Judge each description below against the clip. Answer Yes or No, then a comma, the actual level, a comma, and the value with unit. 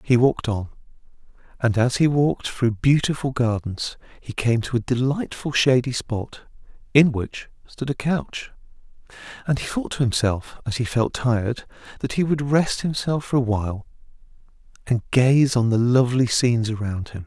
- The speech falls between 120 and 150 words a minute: No, average, 165 wpm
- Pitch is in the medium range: No, low, 125 Hz